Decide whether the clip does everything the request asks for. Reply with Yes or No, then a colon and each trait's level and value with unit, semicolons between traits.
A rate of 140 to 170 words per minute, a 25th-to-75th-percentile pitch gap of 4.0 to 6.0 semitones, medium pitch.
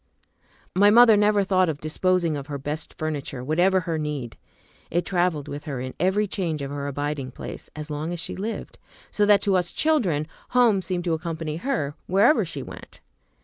No: average, 190 wpm; average, 4.7 semitones; medium, 165 Hz